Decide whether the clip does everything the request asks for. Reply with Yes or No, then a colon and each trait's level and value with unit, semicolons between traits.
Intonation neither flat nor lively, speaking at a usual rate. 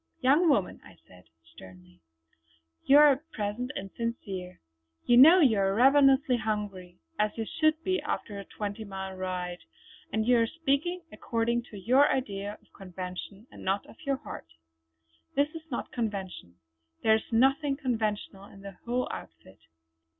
No: wide, 5.8 semitones; average, 155 wpm